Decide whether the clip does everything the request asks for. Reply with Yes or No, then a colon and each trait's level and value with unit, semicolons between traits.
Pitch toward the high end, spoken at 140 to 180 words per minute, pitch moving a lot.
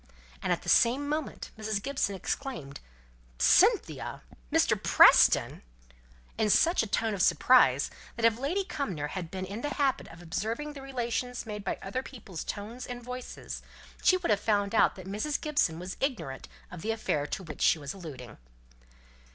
Yes: high, 220 Hz; average, 170 wpm; wide, 6.0 semitones